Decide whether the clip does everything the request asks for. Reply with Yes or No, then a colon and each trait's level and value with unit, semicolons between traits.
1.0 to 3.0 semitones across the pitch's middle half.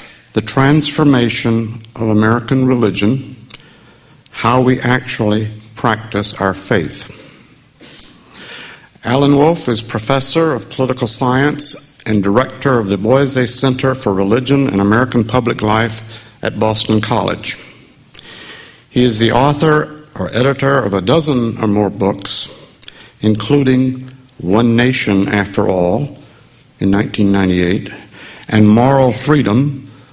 No: average, 3.7 semitones